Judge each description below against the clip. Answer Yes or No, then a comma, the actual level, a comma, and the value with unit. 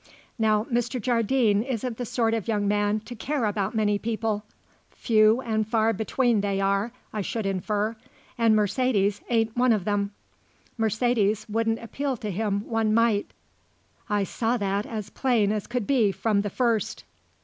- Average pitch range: No, narrow, 2.2 semitones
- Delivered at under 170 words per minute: Yes, average, 160 wpm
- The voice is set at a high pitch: Yes, high, 220 Hz